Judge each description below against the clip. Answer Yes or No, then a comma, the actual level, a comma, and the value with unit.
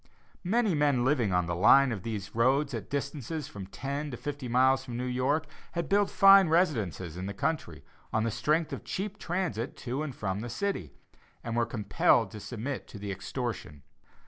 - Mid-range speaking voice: No, low, 130 Hz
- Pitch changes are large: Yes, wide, 5.9 semitones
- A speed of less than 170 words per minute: No, average, 195 wpm